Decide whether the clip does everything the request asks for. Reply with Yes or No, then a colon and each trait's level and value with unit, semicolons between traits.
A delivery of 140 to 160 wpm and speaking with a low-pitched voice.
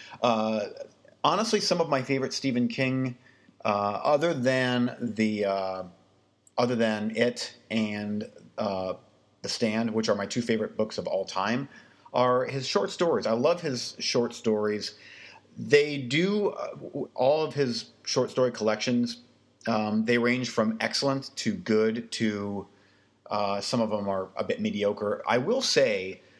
Yes: average, 150 wpm; low, 115 Hz